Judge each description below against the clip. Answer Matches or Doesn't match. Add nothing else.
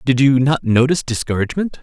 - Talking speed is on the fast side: Doesn't match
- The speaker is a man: Matches